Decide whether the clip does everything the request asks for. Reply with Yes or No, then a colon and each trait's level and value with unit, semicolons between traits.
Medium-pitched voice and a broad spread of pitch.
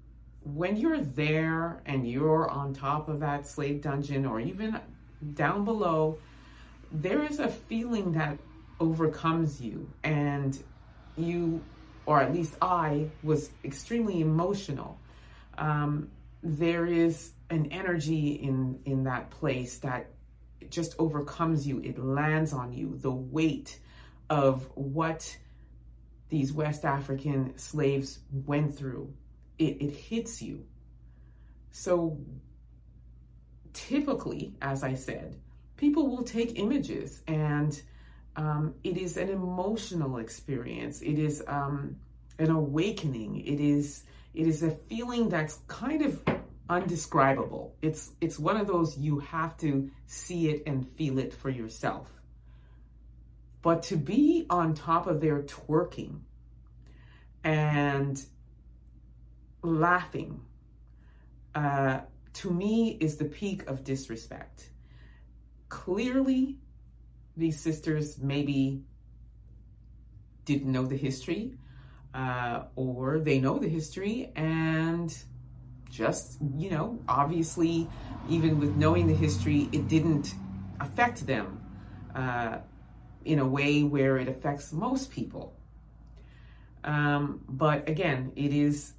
No: medium, 145 Hz; average, 4.3 semitones